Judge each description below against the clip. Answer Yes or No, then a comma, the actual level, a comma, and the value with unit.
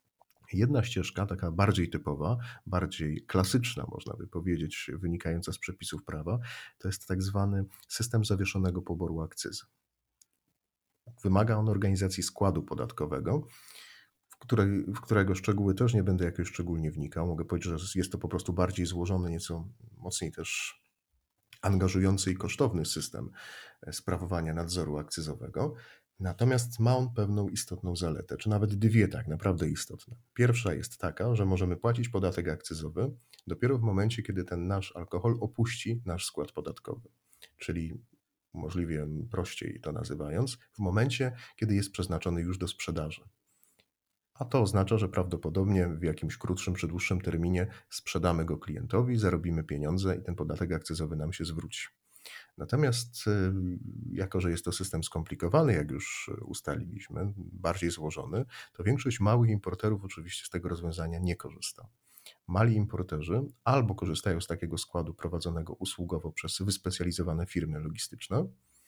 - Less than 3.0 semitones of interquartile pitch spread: No, average, 3.9 semitones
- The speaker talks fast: No, average, 140 wpm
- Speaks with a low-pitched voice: Yes, very low, 90 Hz